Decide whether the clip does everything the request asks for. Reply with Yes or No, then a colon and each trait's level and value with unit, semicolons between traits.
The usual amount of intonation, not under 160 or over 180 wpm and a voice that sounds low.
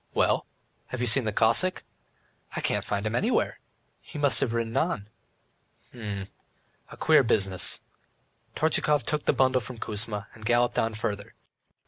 No: average, 3.9 semitones; average, 150 wpm; low, 115 Hz